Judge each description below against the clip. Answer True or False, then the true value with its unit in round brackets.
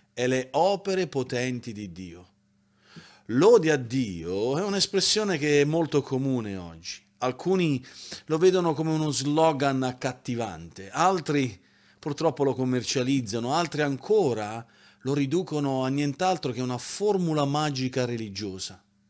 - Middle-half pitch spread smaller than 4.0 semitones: False (5.3 semitones)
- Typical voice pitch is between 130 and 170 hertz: True (135 Hz)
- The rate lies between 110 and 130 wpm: True (120 wpm)